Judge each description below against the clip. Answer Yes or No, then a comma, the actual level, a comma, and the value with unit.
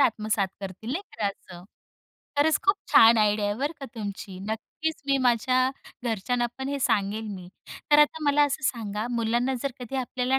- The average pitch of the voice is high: Yes, high, 240 Hz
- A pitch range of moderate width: Yes, average, 4.2 semitones